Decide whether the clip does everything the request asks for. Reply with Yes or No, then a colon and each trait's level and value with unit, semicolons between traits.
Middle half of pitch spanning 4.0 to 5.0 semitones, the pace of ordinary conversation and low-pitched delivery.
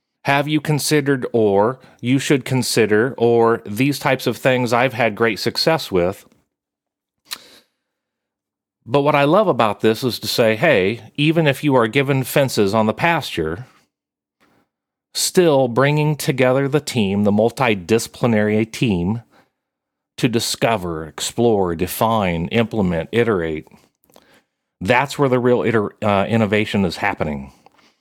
No: average, 4.6 semitones; slow, 120 wpm; low, 115 Hz